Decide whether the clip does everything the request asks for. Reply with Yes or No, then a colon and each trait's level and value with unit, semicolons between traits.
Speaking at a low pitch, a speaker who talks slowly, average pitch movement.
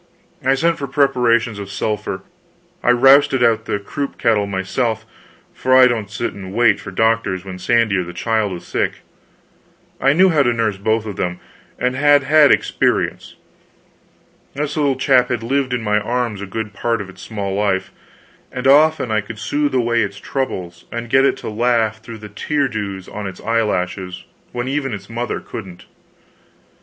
No: low, 115 Hz; average, 185 wpm; average, 4.3 semitones